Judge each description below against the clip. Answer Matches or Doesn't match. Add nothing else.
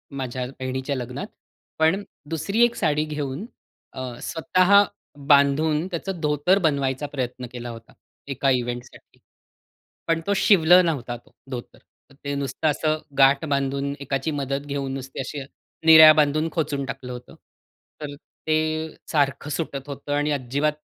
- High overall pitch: Doesn't match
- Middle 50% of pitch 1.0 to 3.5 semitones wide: Matches